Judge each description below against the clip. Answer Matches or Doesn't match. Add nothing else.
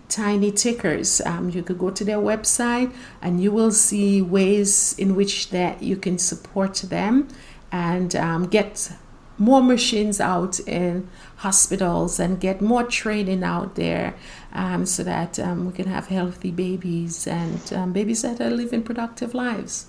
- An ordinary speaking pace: Matches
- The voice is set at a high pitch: Matches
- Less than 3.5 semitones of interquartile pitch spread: Matches